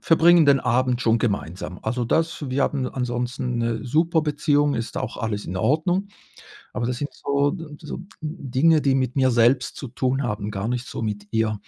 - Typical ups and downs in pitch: Yes, average, 4.0 semitones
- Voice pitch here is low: Yes, low, 125 Hz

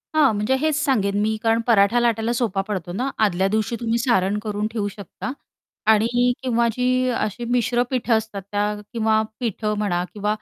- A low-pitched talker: No, high, 220 Hz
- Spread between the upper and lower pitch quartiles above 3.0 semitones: No, average, 2.7 semitones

